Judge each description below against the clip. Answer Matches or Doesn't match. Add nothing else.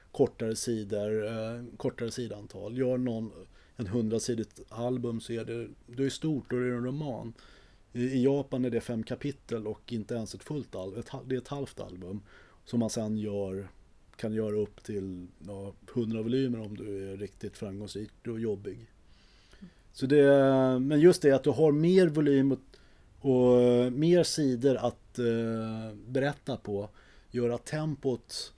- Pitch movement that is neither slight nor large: Matches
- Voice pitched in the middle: Doesn't match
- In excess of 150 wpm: Matches